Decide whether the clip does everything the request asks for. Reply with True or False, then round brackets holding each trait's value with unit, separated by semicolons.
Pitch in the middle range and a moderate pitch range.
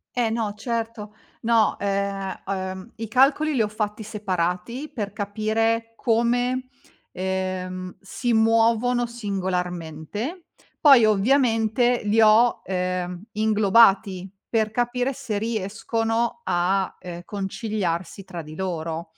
False (215 Hz; 3.6 semitones)